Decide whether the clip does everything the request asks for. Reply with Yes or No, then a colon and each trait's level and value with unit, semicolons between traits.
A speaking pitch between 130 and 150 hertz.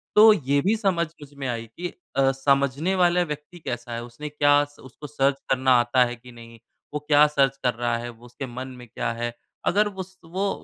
Yes: medium, 140 Hz